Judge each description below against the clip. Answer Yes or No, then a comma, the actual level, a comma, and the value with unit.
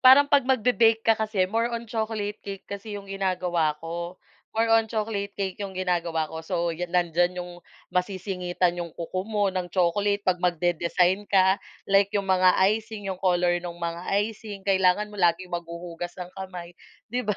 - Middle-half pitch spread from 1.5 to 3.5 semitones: Yes, average, 2.8 semitones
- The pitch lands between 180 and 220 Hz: Yes, medium, 185 Hz